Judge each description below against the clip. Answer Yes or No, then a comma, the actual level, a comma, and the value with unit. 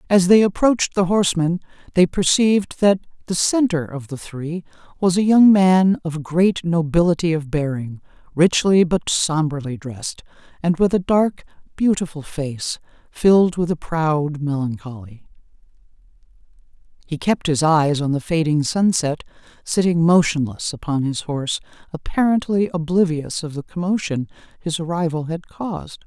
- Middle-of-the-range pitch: Yes, medium, 165 Hz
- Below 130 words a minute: No, slow, 135 wpm